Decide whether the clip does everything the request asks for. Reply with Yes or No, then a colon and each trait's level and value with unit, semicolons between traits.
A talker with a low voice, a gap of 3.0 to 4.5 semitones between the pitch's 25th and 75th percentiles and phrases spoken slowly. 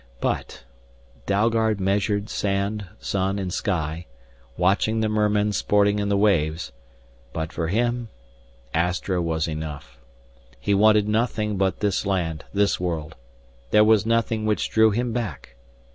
Yes: low, 100 Hz; average, 3.4 semitones; slow, 130 wpm